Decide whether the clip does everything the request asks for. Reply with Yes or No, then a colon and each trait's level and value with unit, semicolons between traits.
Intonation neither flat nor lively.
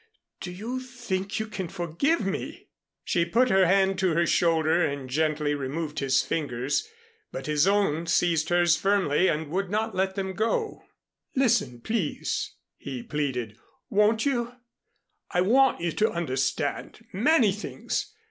No: wide, 5.7 semitones